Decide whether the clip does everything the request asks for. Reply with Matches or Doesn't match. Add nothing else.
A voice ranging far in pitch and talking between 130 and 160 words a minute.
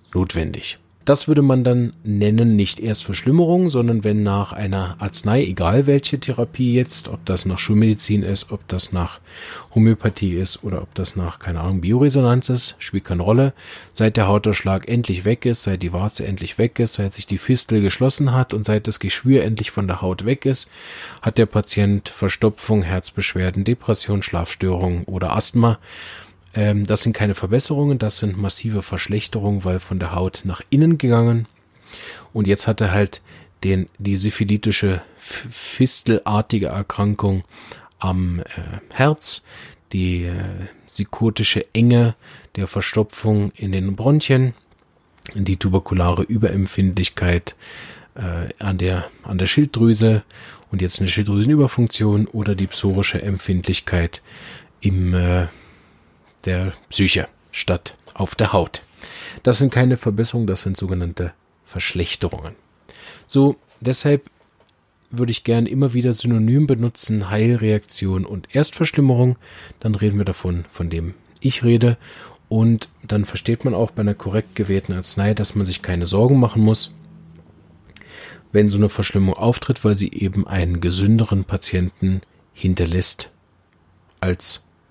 Doesn't match